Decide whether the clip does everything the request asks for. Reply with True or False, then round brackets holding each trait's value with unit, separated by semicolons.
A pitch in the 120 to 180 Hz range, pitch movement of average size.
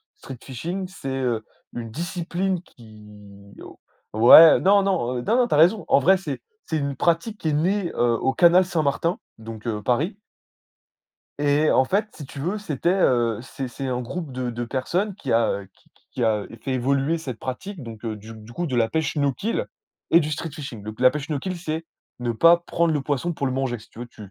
False (140 Hz; 6.1 semitones)